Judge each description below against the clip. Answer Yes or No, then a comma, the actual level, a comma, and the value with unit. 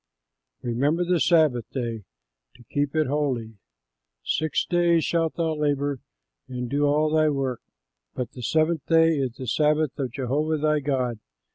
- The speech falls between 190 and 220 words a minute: No, average, 150 wpm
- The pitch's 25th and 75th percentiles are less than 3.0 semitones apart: No, average, 3.7 semitones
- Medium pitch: Yes, medium, 145 Hz